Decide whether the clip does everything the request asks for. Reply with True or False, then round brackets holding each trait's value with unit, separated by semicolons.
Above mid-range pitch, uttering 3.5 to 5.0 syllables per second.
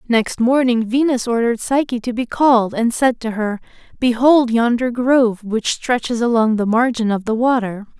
True (235 Hz; 4.9 syllables/s)